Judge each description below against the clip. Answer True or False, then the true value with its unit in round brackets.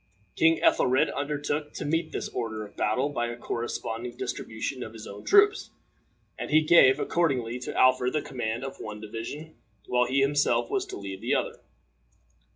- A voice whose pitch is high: False (130 Hz)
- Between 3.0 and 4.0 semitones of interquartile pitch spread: False (4.5 semitones)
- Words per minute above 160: True (170 wpm)